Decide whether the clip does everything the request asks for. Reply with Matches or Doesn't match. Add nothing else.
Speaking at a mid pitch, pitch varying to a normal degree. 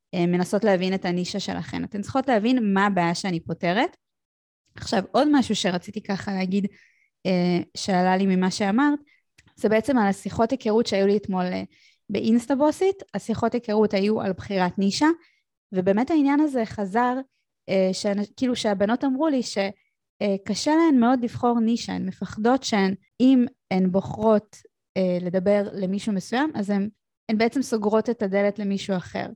Doesn't match